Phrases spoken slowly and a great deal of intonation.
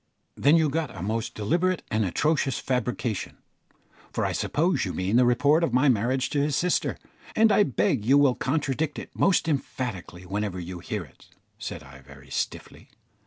No: average, 175 wpm; wide, 6.7 semitones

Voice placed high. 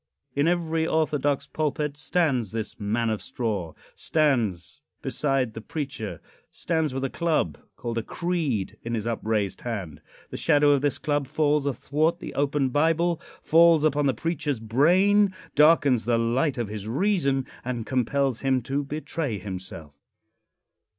No: medium, 140 Hz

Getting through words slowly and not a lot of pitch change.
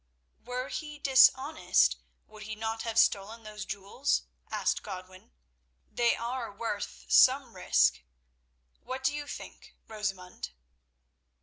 No: slow, 115 wpm; average, 4.5 semitones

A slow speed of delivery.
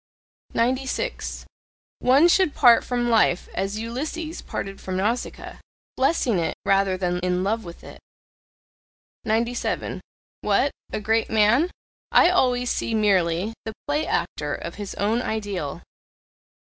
Yes: slow, 125 wpm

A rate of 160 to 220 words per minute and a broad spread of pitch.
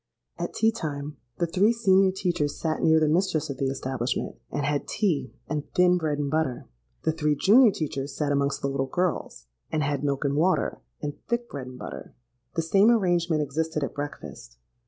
No: average, 190 wpm; average, 4.1 semitones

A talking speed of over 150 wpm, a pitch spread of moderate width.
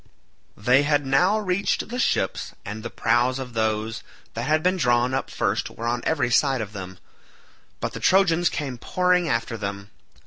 No: average, 175 wpm; wide, 6.2 semitones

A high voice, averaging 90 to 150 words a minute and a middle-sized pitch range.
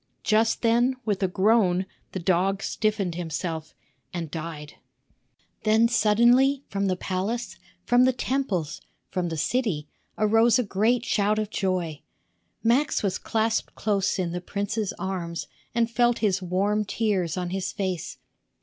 Yes: high, 200 Hz; average, 140 wpm; average, 4.0 semitones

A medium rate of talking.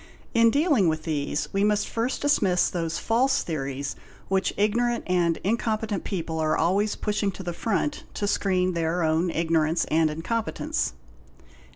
Yes: average, 150 wpm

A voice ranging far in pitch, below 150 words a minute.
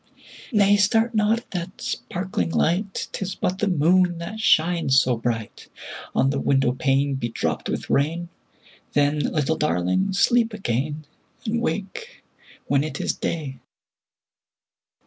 Yes: wide, 6.2 semitones; slow, 135 wpm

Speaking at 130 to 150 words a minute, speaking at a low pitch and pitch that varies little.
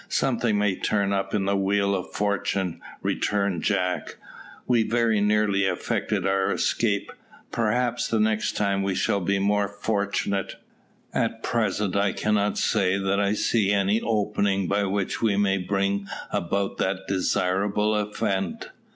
Yes: average, 140 wpm; low, 100 Hz; narrow, 1.3 semitones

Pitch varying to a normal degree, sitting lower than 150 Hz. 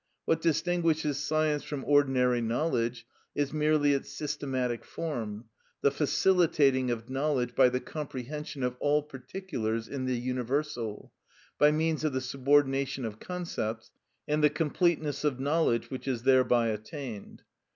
Yes: average, 3.4 semitones; medium, 140 Hz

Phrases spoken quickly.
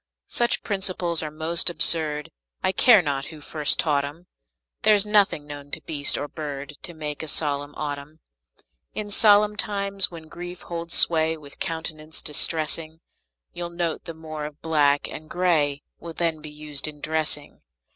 No: average, 160 wpm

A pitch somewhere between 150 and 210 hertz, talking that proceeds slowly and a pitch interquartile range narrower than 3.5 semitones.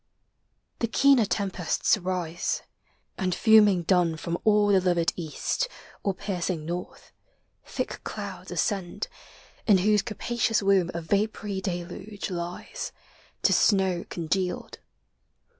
Yes: high, 190 Hz; slow, 110 wpm; average, 3.1 semitones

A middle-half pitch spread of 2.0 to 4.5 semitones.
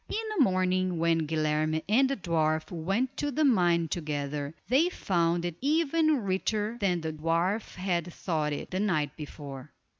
No: average, 5.2 semitones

